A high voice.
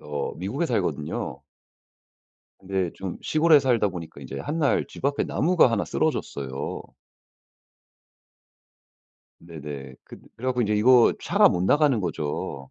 No: very low, 95 Hz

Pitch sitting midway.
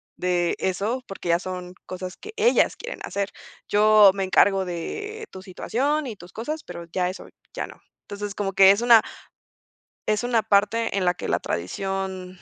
No: high, 195 Hz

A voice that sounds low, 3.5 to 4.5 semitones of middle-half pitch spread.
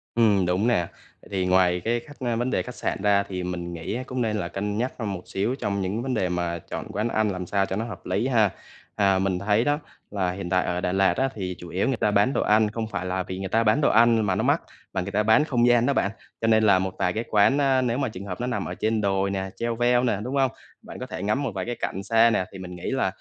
Yes: low, 105 Hz; average, 4.0 semitones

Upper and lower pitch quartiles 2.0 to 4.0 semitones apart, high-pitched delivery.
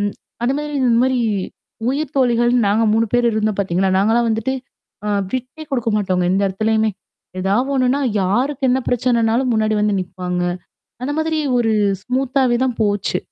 Yes: average, 3.7 semitones; high, 235 Hz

